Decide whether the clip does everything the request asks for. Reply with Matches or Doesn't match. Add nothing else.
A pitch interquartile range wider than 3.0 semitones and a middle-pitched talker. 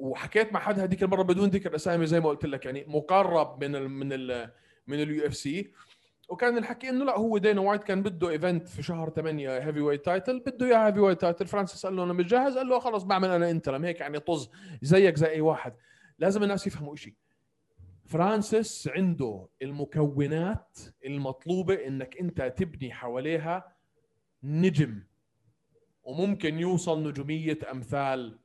Matches